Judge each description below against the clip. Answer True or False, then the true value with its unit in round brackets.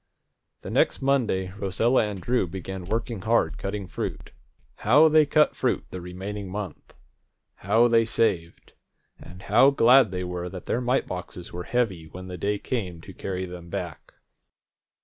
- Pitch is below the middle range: True (100 Hz)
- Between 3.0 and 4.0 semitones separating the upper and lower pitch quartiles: False (4.5 semitones)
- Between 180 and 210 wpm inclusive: False (160 wpm)